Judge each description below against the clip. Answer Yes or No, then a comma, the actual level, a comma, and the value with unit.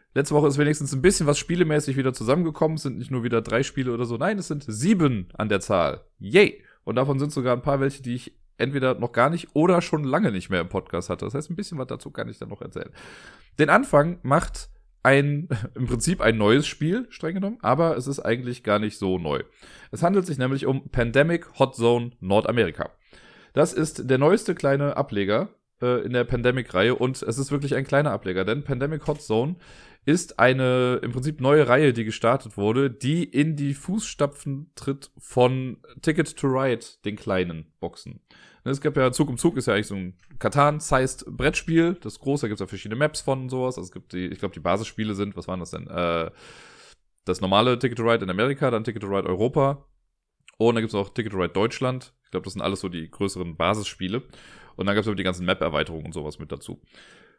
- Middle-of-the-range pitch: No, low, 130 Hz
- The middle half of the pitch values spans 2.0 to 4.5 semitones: No, average, 5.1 semitones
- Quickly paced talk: Yes, fast, 220 wpm